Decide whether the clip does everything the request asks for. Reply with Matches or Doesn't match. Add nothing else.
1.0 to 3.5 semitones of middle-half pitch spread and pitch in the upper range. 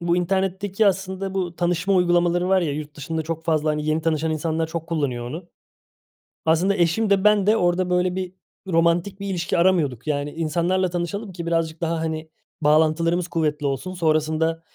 Doesn't match